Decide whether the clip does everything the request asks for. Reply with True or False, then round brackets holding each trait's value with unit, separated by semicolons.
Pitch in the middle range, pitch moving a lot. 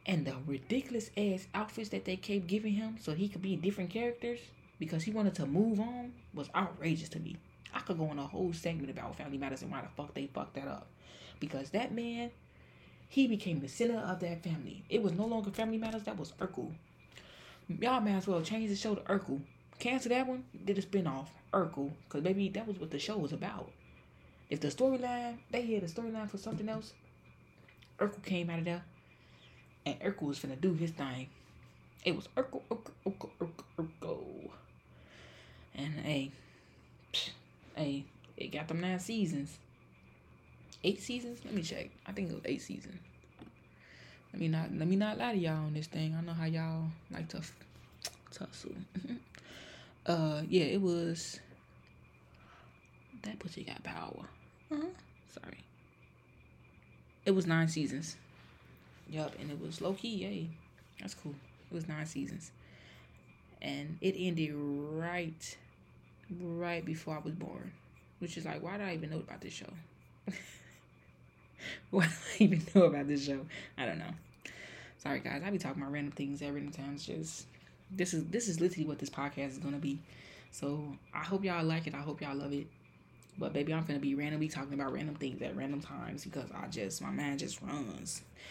True (160 Hz; 5.7 semitones)